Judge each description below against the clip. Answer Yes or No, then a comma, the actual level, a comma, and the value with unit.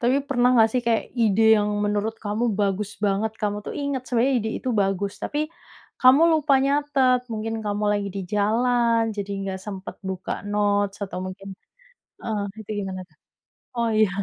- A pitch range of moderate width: Yes, average, 3.1 semitones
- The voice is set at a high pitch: Yes, high, 210 Hz